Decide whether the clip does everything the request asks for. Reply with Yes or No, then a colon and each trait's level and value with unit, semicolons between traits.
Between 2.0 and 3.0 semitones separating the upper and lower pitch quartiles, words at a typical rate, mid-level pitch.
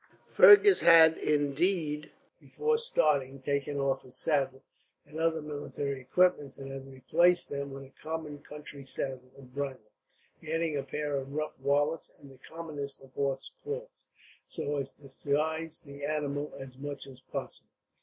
Yes: average, 2.7 semitones; average, 155 wpm; medium, 145 Hz